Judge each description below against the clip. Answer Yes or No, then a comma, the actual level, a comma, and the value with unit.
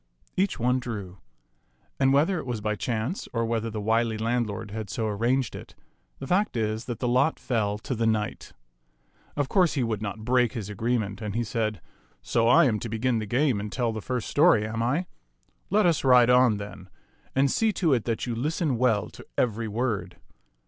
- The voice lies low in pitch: Yes, low, 115 Hz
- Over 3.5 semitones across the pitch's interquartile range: No, average, 3.0 semitones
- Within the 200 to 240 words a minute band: Yes, fast, 205 wpm